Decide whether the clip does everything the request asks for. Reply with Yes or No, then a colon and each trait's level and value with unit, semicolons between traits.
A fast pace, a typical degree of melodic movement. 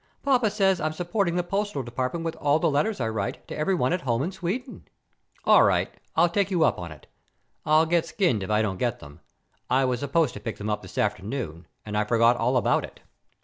No: fast, 225 wpm; wide, 7.9 semitones